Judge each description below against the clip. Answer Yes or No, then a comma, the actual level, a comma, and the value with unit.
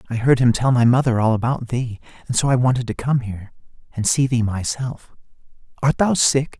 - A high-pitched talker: No, low, 125 Hz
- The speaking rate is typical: No, fast, 210 wpm